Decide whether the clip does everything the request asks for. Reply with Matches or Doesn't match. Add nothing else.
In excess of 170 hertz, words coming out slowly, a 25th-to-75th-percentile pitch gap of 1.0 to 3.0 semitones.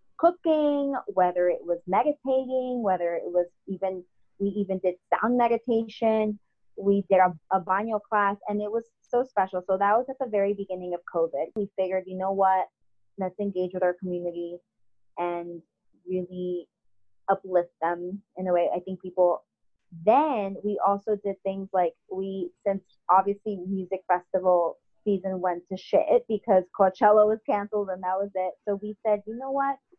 Doesn't match